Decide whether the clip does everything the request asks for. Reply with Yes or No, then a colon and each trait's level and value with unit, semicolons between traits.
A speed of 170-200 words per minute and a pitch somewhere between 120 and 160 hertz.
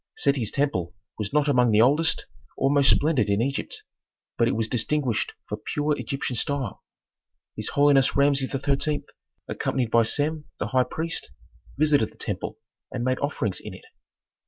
No: average, 160 wpm; low, 135 Hz